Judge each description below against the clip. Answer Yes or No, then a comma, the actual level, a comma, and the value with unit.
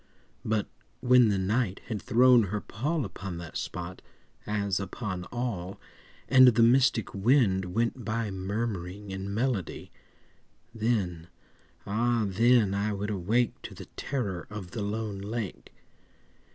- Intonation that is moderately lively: Yes, average, 3.6 semitones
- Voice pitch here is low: Yes, low, 105 Hz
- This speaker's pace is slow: Yes, slow, 125 wpm